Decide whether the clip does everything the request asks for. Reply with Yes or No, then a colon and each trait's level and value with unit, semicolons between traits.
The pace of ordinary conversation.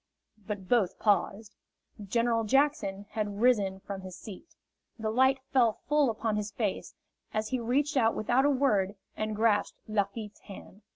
Yes: average, 155 wpm